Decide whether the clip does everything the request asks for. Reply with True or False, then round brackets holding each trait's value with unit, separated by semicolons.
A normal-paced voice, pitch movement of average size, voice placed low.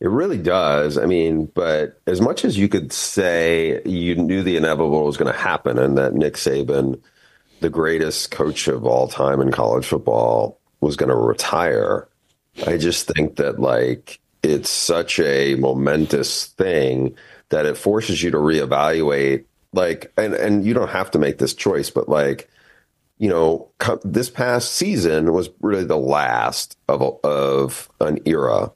True (165 wpm; 4.3 semitones; 80 Hz)